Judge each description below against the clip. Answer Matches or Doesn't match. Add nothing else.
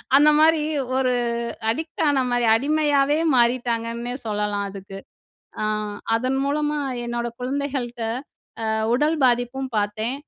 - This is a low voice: Doesn't match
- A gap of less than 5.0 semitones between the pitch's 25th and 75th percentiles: Matches